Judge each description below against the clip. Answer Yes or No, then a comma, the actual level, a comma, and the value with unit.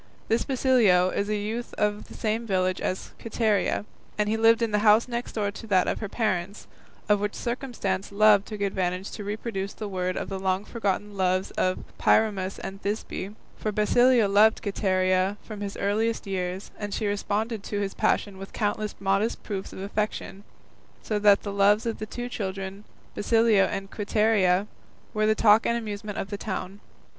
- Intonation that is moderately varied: No, narrow, 2.0 semitones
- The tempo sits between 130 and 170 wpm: No, average, 185 wpm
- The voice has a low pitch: No, high, 205 Hz